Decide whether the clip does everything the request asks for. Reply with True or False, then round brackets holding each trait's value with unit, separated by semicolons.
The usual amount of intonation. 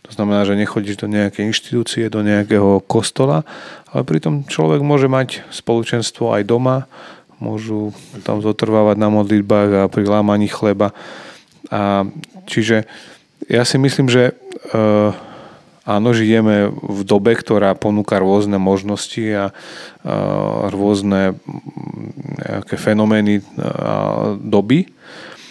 False (2.2 semitones)